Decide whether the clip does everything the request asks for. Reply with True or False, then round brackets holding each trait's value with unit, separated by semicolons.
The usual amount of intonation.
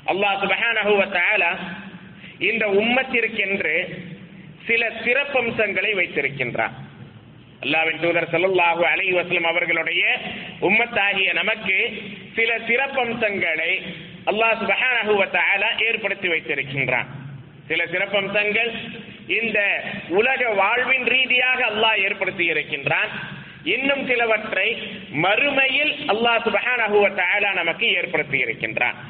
True (4.8 semitones)